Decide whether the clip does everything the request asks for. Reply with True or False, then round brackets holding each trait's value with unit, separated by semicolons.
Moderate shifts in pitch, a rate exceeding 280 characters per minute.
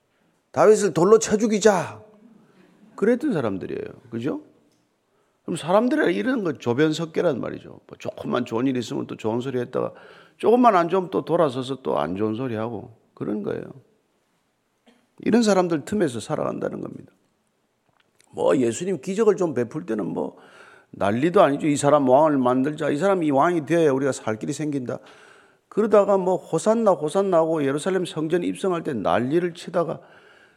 False (6.4 semitones; 330 characters per minute)